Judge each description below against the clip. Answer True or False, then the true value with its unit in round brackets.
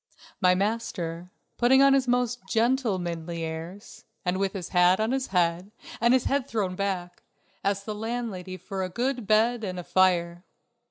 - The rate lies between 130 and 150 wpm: False (165 wpm)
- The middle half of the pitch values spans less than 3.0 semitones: False (4.9 semitones)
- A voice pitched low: False (195 Hz)